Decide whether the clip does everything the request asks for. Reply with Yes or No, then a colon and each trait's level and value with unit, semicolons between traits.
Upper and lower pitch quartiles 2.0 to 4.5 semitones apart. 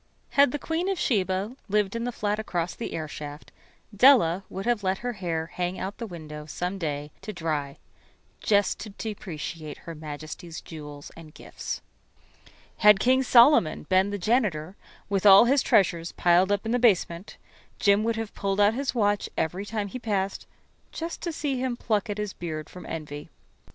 No: average, 5.3 semitones